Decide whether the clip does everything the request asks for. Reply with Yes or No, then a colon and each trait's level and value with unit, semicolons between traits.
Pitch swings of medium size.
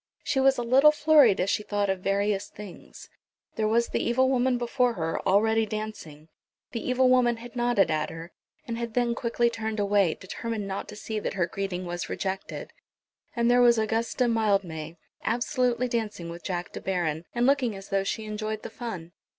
Yes: average, 3.7 semitones